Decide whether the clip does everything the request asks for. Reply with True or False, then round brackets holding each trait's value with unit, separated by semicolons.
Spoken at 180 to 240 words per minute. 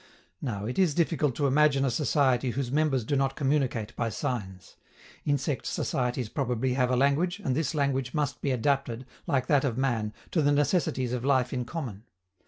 True (185 wpm)